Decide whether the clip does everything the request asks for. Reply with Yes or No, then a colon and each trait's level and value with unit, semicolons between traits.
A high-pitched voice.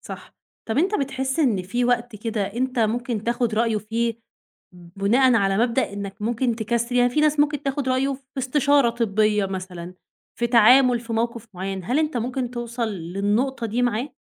Yes: high, 235 Hz